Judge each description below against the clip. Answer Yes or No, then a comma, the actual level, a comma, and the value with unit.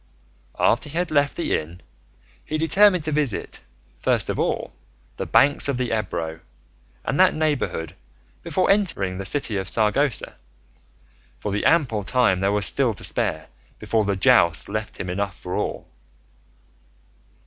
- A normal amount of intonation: No, wide, 7.2 semitones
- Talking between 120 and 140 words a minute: No, average, 150 wpm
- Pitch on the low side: Yes, low, 110 Hz